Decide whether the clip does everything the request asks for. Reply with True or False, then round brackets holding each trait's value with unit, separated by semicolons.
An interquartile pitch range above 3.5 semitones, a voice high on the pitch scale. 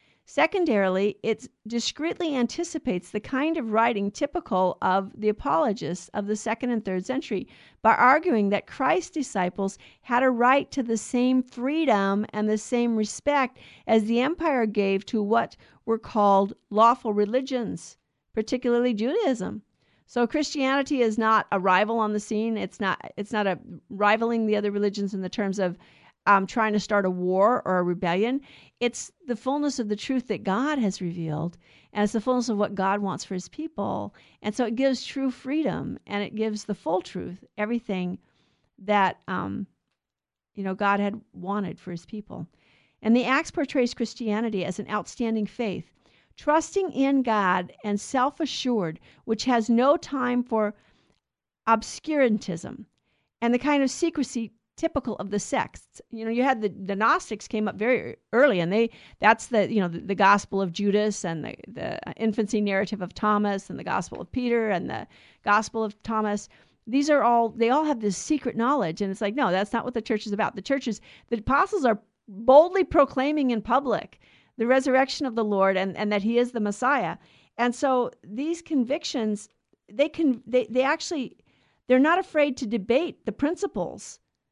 True (4.0 semitones; 225 Hz)